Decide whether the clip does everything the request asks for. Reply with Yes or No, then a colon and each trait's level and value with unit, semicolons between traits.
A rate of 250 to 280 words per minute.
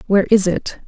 No: fast, 205 wpm